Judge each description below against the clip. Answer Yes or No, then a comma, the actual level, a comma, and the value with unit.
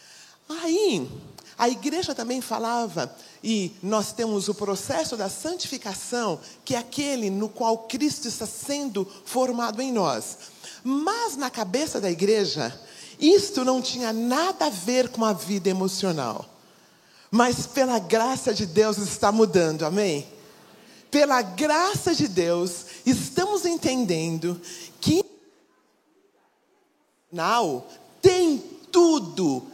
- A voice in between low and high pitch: No, high, 235 Hz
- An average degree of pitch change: No, wide, 6.1 semitones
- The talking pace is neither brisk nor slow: No, slow, 115 wpm